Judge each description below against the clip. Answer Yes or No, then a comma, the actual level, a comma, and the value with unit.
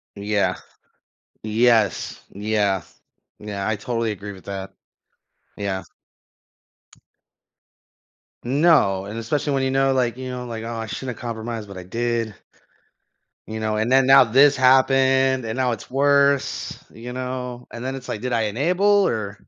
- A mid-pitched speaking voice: No, low, 120 Hz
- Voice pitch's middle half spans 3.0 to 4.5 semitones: Yes, average, 3.7 semitones